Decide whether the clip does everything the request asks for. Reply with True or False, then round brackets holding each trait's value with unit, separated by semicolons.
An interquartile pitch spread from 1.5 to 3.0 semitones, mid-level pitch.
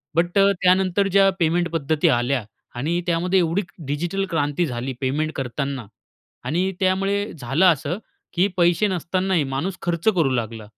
False (5.0 semitones; 170 Hz)